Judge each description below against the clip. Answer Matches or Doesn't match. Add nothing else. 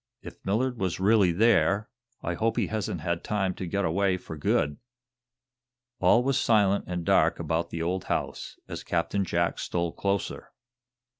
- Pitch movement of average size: Matches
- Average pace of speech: Matches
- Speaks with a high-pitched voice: Doesn't match